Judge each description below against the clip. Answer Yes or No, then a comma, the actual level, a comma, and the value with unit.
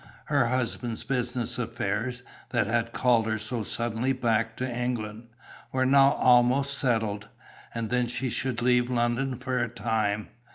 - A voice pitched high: No, low, 120 Hz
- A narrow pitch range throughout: Yes, narrow, 2.0 semitones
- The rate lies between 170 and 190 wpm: No, average, 150 wpm